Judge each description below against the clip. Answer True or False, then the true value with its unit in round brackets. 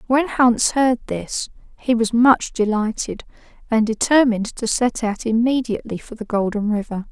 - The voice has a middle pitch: False (230 Hz)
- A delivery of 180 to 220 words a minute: False (150 wpm)